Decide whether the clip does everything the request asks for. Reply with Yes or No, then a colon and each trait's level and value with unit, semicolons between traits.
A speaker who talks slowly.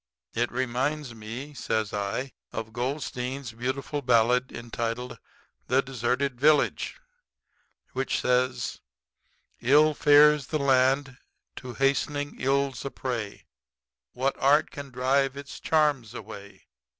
Yes: slow, 110 wpm